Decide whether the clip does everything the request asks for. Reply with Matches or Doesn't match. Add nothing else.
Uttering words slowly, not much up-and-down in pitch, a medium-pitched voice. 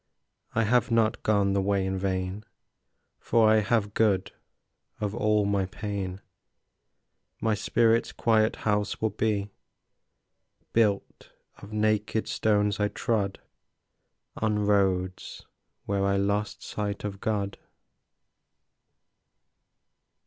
Doesn't match